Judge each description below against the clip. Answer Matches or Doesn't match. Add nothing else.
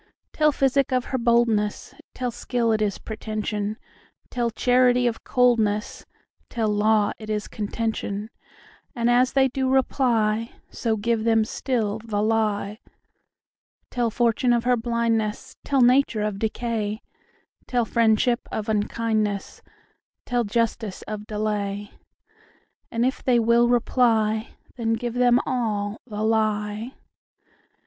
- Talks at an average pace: Doesn't match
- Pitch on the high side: Matches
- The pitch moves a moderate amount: Doesn't match